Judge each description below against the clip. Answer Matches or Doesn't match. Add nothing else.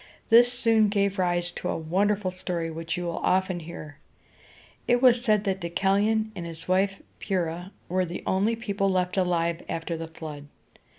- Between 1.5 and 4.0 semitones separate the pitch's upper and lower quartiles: Matches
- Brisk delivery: Doesn't match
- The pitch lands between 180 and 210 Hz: Matches